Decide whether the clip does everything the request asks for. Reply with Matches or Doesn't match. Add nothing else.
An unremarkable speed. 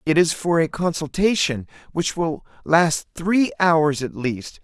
Matches